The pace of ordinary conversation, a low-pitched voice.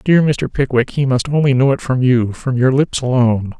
No: fast, 215 wpm; low, 130 Hz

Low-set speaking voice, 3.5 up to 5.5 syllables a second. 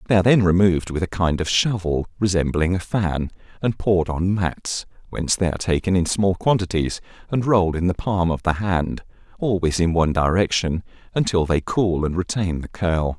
Yes: very low, 90 Hz; 5.3 syllables/s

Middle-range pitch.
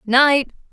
No: very high, 260 Hz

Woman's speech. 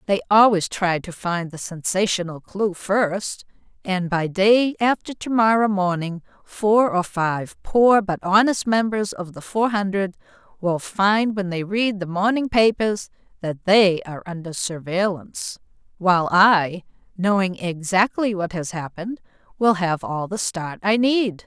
Yes: female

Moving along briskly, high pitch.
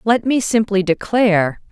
No: average, 140 wpm; high, 210 Hz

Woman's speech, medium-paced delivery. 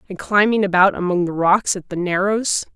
Yes: female; average, 195 wpm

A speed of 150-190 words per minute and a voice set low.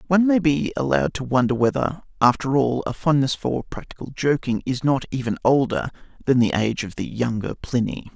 Yes: average, 185 wpm; low, 130 Hz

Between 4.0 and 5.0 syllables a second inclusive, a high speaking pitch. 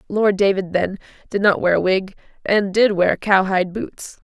Yes: 4.7 syllables/s; high, 195 Hz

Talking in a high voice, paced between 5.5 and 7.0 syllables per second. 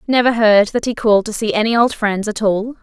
Yes: high, 220 Hz; 5.7 syllables/s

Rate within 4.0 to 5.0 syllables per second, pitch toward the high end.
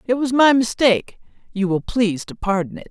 No: 5.7 syllables/s; high, 220 Hz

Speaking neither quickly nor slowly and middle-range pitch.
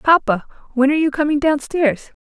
No: average, 190 wpm; very high, 280 Hz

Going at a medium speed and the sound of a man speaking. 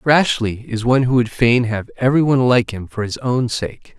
No: fast, 225 wpm; male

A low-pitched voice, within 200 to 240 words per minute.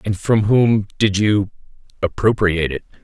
No: low, 100 Hz; average, 140 wpm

